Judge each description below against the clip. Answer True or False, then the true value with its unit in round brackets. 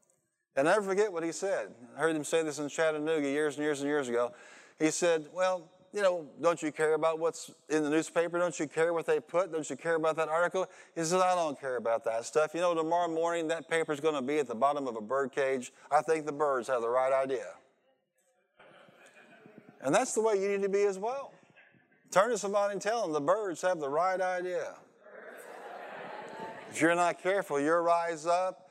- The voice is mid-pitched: True (165 Hz)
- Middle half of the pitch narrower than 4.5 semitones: True (3.2 semitones)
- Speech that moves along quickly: True (220 wpm)